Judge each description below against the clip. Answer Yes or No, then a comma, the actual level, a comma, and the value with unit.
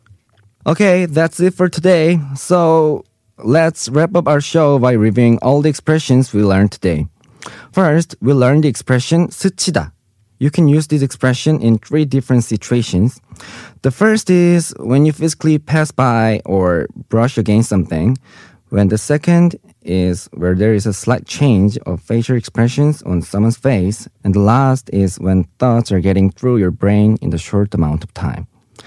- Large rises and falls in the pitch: Yes, wide, 6.8 semitones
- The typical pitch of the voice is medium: No, low, 125 Hz